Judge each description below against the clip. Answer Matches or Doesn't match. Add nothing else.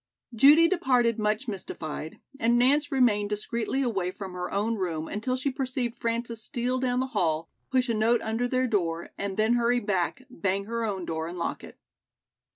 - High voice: Matches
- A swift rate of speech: Doesn't match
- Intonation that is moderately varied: Matches